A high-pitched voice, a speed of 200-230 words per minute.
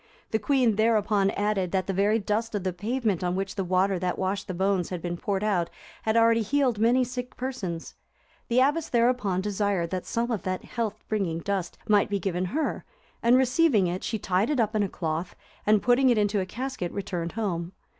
Yes: high, 205 Hz; fast, 205 wpm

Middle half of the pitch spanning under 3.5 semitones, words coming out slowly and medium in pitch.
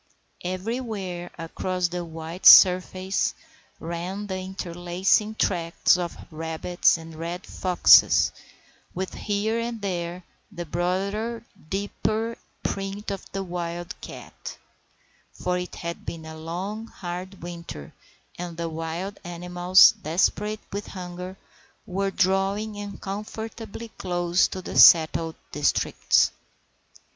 Yes: narrow, 2.5 semitones; slow, 110 wpm; medium, 180 Hz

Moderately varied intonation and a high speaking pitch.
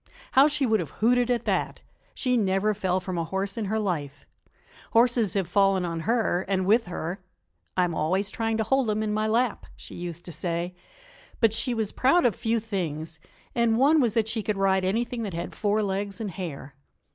Yes: average, 3.8 semitones; high, 205 Hz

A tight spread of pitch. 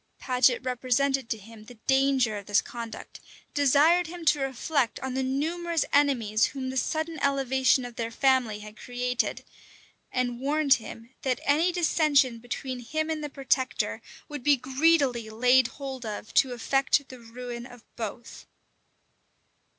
No: average, 3.0 semitones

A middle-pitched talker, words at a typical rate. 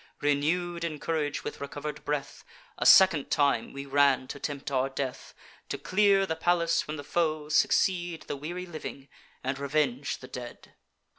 Yes: medium, 150 Hz; average, 160 wpm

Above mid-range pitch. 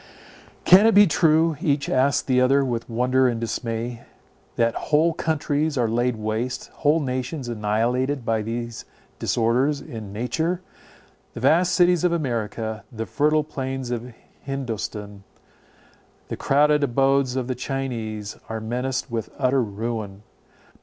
No: low, 125 Hz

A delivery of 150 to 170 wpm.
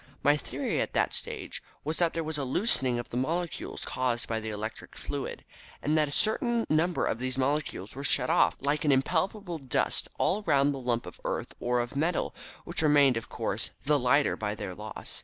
No: fast, 205 wpm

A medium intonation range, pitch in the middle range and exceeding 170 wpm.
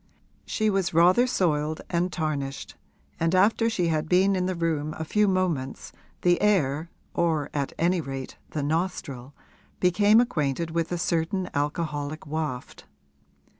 No: average, 3.8 semitones; medium, 165 Hz; average, 140 wpm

